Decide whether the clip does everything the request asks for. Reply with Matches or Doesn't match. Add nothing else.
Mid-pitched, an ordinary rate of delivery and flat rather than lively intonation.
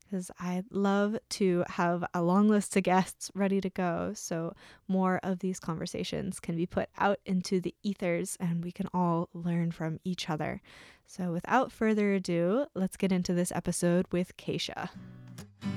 Matches